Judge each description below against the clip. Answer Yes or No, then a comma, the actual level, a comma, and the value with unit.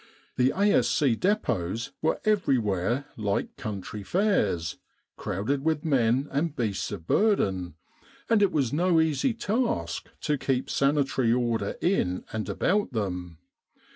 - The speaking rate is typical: No, slow, 125 wpm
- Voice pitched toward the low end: Yes, low, 130 Hz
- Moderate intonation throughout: No, wide, 8.8 semitones